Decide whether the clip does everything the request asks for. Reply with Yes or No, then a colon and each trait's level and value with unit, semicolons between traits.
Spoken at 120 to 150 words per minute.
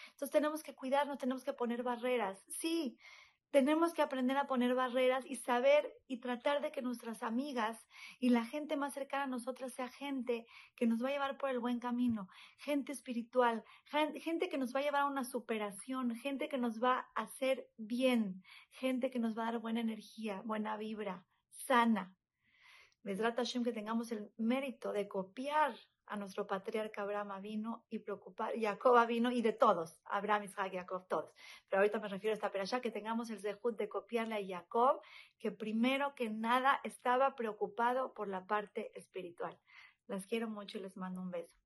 No: average, 185 wpm